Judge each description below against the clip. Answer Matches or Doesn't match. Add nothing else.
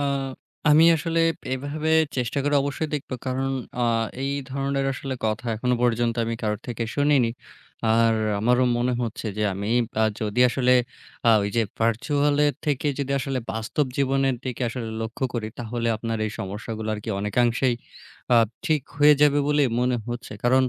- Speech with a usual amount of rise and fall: Matches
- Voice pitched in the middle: Doesn't match